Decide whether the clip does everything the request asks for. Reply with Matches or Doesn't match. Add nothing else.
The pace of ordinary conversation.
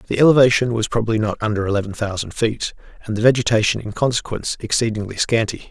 Matches